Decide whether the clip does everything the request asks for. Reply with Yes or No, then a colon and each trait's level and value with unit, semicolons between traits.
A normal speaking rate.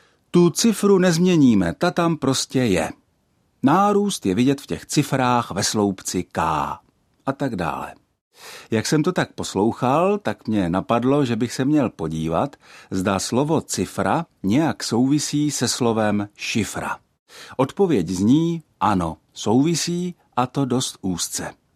Yes: average, 130 wpm